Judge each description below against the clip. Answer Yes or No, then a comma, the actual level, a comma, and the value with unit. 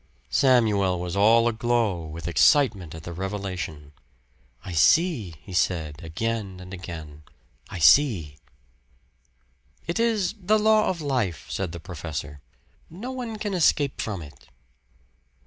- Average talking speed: No, slow, 130 wpm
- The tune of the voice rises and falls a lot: Yes, wide, 9.0 semitones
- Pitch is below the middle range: Yes, very low, 95 Hz